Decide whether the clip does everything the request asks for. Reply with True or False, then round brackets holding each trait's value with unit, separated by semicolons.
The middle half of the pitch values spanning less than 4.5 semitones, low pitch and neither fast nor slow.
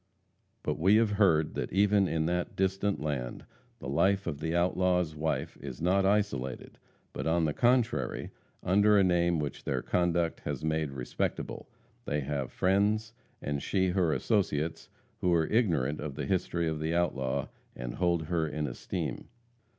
True (4.1 semitones; 85 Hz; 160 wpm)